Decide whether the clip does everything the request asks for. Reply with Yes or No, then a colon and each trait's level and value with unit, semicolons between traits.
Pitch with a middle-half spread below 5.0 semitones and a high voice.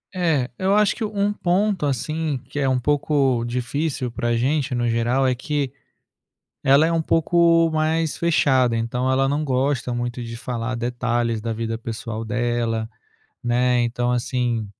No: average, 4.2 semitones; low, 125 Hz